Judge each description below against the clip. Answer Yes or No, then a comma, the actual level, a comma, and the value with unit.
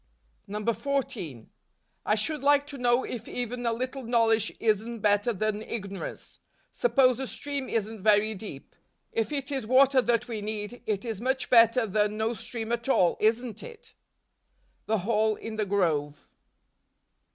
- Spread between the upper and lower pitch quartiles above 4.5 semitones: No, average, 3.0 semitones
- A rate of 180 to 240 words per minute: No, average, 150 wpm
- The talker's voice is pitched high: Yes, high, 225 Hz